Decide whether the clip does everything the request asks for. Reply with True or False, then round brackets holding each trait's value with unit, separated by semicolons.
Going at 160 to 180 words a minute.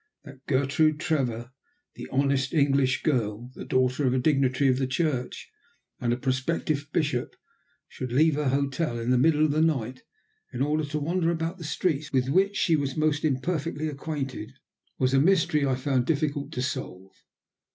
True (170 wpm)